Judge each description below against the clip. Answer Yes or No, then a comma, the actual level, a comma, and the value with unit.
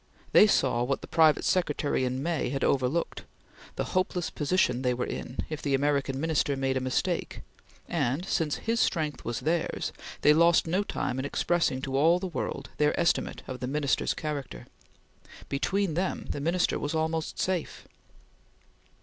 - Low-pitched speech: No, medium, 150 Hz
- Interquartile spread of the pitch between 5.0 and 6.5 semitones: No, average, 4.1 semitones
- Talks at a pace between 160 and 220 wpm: Yes, average, 165 wpm